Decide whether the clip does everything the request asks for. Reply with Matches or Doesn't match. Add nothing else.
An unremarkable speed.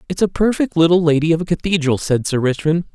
Doesn't match